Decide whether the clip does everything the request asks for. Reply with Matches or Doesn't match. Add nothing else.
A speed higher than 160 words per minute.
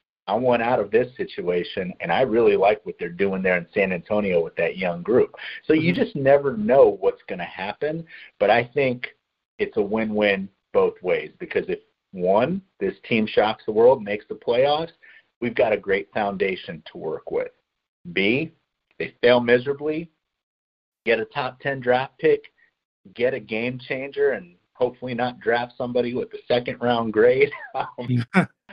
Matches